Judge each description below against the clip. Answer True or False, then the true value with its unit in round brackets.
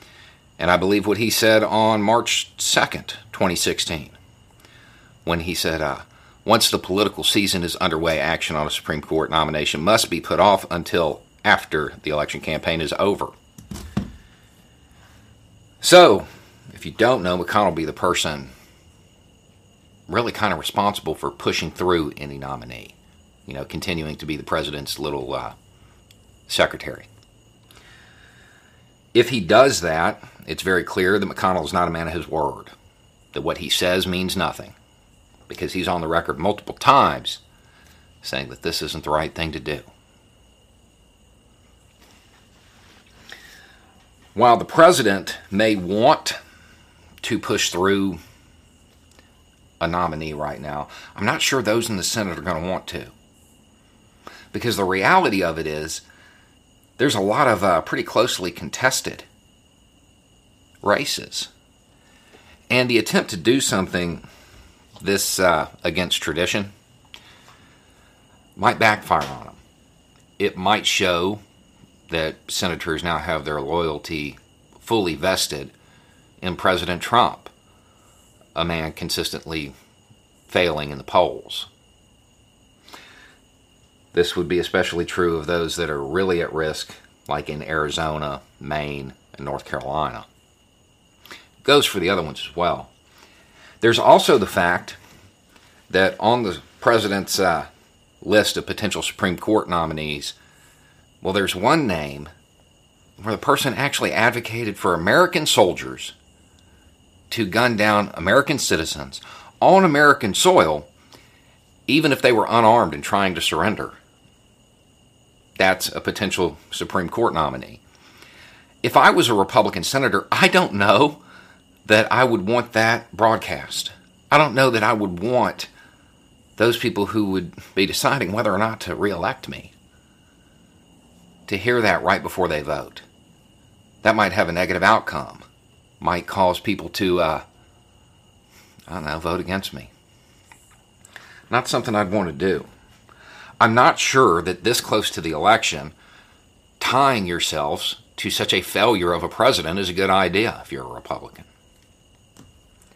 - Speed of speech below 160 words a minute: True (135 wpm)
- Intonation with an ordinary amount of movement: True (4.4 semitones)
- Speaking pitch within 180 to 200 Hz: False (95 Hz)